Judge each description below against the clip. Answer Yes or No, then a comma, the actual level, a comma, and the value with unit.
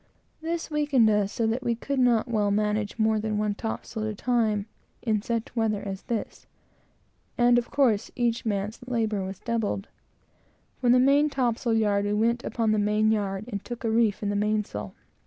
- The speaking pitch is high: Yes, high, 220 Hz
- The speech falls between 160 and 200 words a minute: Yes, average, 185 wpm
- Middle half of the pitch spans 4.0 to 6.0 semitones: No, narrow, 2.5 semitones